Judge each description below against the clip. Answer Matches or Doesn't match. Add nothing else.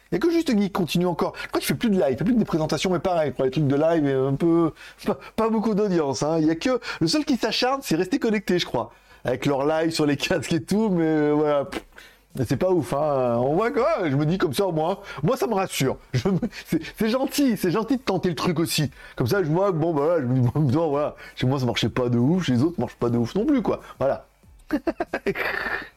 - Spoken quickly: Matches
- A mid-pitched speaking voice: Matches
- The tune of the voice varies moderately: Doesn't match